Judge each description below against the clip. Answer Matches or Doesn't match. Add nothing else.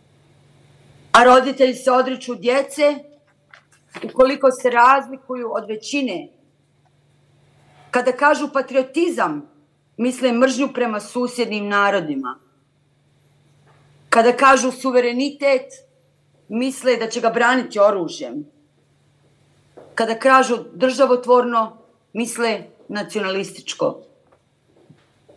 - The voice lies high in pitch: Matches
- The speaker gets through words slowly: Matches